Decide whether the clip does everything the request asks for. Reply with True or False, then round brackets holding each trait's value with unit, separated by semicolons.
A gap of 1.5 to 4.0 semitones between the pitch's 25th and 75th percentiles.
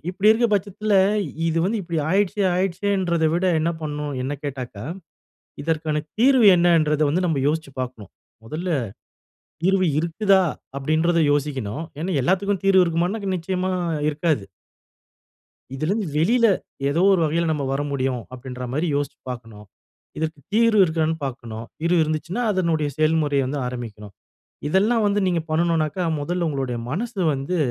False (4.6 semitones)